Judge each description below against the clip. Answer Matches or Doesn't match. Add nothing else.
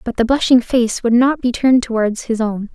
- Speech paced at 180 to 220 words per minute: Doesn't match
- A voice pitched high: Matches